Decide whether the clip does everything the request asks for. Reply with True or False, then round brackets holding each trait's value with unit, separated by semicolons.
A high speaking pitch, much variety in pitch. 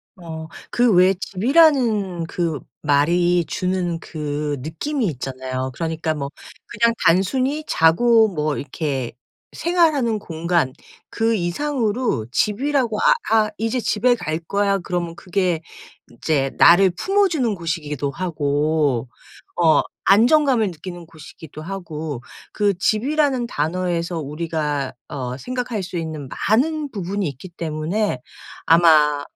False (175 Hz; 6.3 semitones)